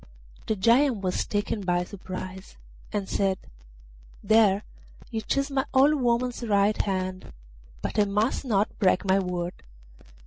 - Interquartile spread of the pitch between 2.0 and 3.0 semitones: No, average, 3.8 semitones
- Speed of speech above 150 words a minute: No, slow, 135 wpm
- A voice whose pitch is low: No, high, 205 Hz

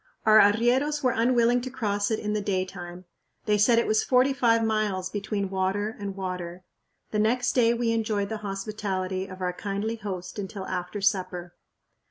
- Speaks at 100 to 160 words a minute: No, average, 175 wpm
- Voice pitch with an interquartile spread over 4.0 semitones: No, average, 3.2 semitones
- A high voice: Yes, high, 205 Hz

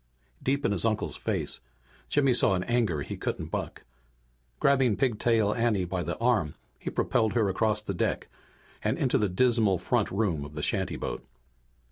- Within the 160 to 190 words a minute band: Yes, average, 165 wpm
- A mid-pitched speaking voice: No, low, 105 Hz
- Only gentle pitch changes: No, average, 4.3 semitones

